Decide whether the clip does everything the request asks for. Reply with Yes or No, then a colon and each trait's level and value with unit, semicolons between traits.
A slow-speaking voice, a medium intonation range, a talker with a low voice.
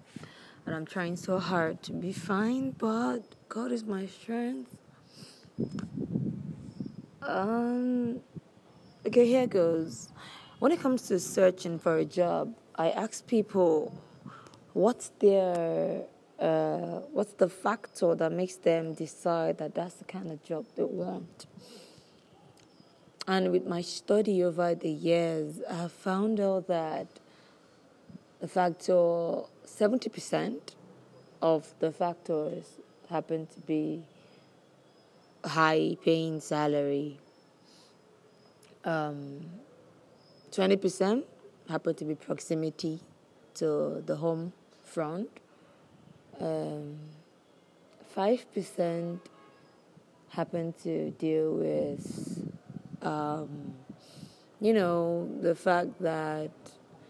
No: slow, 100 wpm; average, 3.2 semitones; medium, 170 Hz